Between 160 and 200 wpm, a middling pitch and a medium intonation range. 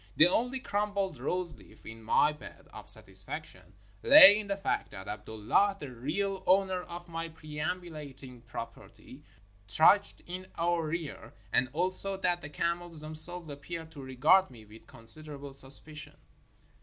No: average, 140 wpm; medium, 160 Hz; average, 4.9 semitones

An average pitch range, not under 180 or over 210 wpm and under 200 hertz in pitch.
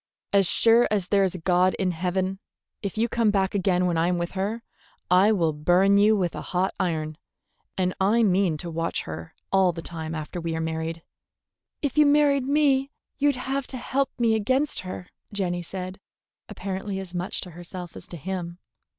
Yes: average, 3.8 semitones; average, 185 wpm; high, 190 Hz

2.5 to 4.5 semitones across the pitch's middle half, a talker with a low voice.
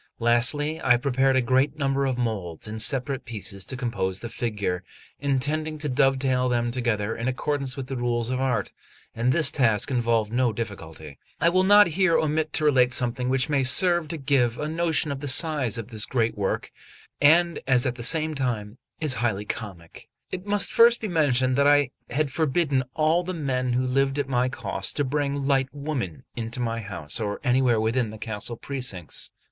Yes: average, 3.8 semitones; low, 130 Hz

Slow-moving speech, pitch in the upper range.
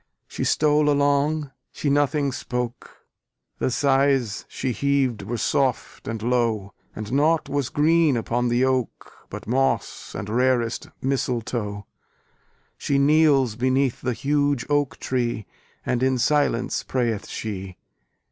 No: slow, 125 wpm; low, 130 Hz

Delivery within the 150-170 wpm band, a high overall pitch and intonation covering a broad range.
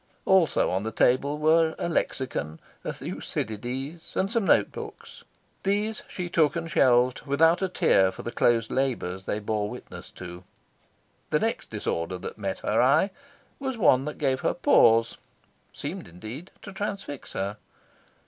No: average, 155 wpm; low, 135 Hz; wide, 7.8 semitones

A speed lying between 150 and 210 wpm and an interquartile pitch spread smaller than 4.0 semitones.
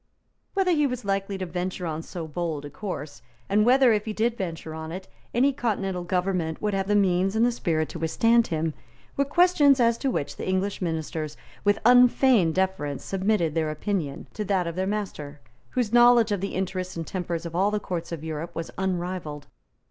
No: average, 200 wpm; average, 4.8 semitones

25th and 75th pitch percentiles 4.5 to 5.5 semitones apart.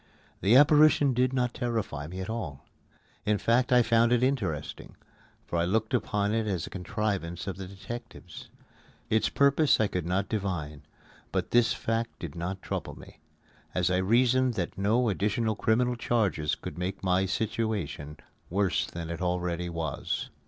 Yes: average, 4.8 semitones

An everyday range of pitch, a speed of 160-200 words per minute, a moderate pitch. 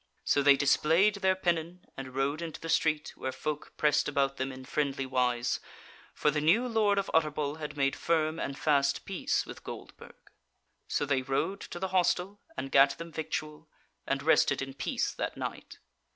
Yes: average, 3.6 semitones; average, 180 wpm; medium, 150 Hz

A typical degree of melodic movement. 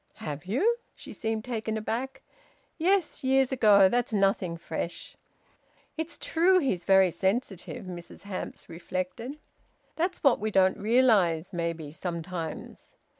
No: wide, 6.4 semitones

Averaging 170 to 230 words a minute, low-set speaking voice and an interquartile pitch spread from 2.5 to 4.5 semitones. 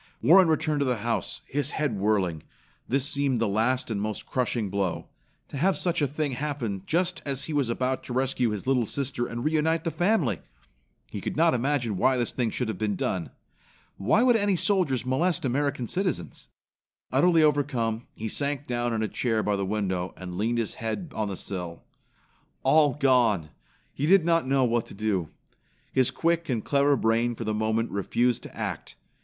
No: average, 190 wpm; low, 125 Hz; average, 5.1 semitones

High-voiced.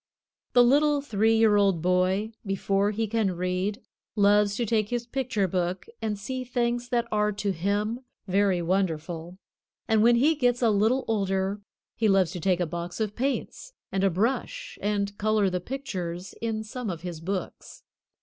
Yes: high, 205 Hz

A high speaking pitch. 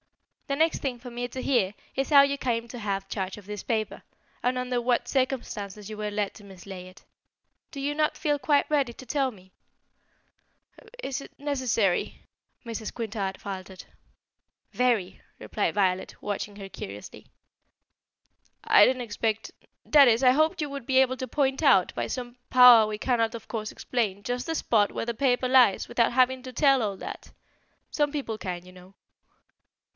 Yes: high, 240 Hz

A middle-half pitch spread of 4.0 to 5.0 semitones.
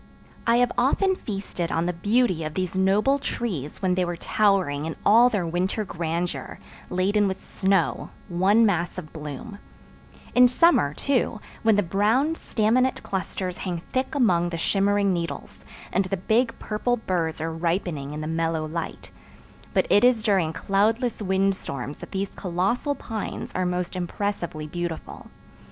Yes: average, 4.3 semitones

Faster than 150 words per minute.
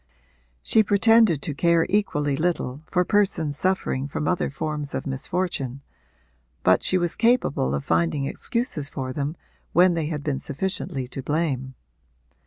No: average, 145 wpm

